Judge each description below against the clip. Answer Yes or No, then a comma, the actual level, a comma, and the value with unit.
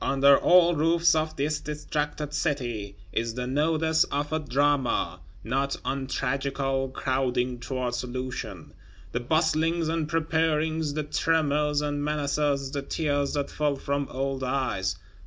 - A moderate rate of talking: No, slow, 130 wpm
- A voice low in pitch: No, medium, 145 Hz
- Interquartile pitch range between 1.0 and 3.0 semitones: Yes, average, 2.7 semitones